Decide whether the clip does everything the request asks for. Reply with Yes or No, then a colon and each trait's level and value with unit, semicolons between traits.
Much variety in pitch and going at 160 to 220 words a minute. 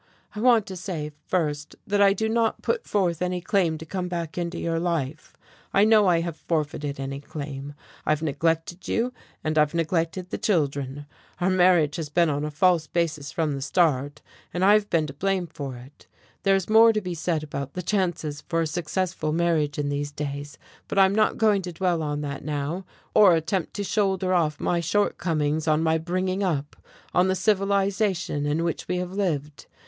No: average, 4.0 semitones; average, 195 wpm